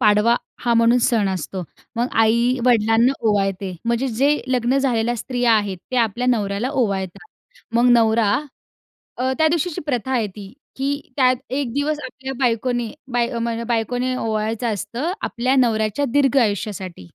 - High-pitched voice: Yes, high, 235 Hz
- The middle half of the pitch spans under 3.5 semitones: Yes, average, 3.0 semitones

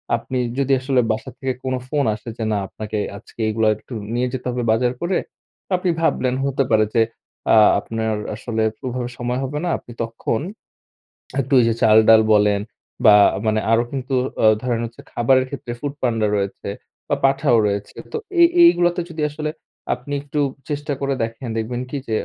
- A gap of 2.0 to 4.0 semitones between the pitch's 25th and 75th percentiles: Yes, average, 3.6 semitones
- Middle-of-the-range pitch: No, low, 125 Hz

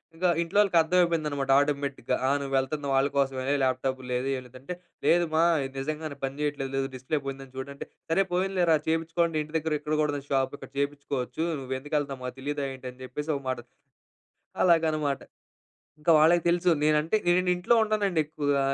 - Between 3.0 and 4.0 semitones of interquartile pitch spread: Yes, average, 3.3 semitones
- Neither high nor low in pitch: Yes, medium, 145 Hz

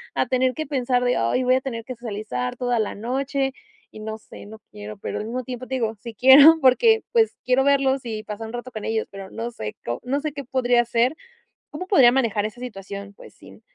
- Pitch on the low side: No, high, 245 Hz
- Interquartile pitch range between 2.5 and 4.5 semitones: Yes, average, 3.4 semitones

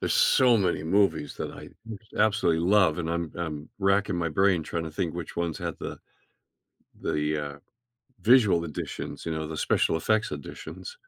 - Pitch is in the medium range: No, very low, 85 Hz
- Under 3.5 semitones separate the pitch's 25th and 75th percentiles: No, average, 4.1 semitones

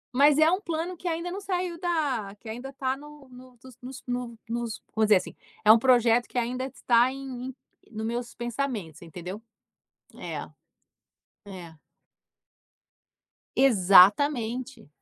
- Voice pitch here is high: Yes, very high, 250 Hz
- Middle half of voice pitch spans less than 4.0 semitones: No, average, 4.3 semitones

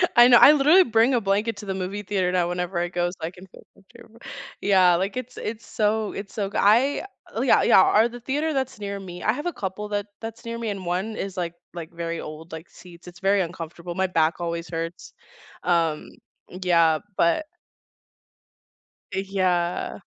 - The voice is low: No, high, 190 Hz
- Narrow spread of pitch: No, average, 4.0 semitones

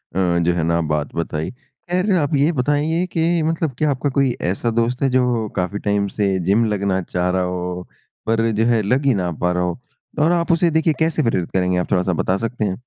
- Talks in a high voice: No, low, 115 Hz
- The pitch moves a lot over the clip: Yes, wide, 8.0 semitones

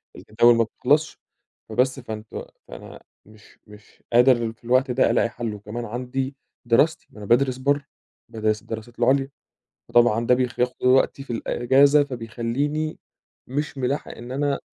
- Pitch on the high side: No, low, 125 Hz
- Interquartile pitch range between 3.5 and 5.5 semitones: No, average, 2.7 semitones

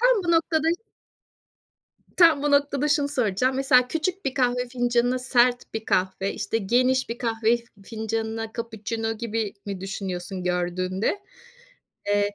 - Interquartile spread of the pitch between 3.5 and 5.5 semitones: Yes, average, 4.6 semitones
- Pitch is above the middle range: Yes, high, 235 Hz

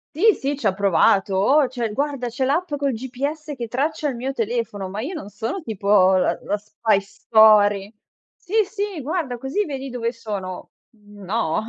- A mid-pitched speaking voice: No, high, 235 Hz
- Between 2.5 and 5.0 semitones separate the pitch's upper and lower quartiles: No, wide, 5.6 semitones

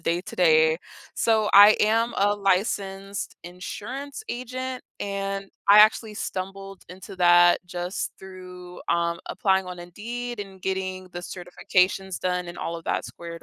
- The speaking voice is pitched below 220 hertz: Yes, high, 190 Hz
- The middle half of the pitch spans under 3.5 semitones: Yes, narrow, 2.5 semitones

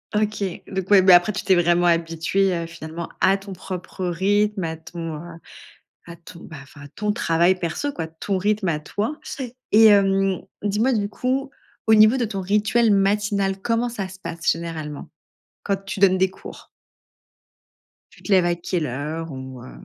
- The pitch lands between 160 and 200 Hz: Yes, high, 190 Hz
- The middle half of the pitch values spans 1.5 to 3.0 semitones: No, average, 3.6 semitones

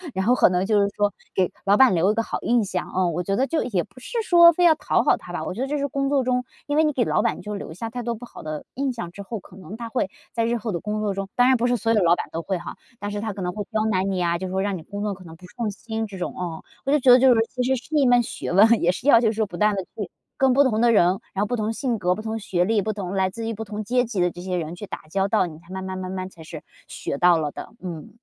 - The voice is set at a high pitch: Yes, high, 210 Hz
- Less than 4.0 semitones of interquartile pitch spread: No, average, 4.5 semitones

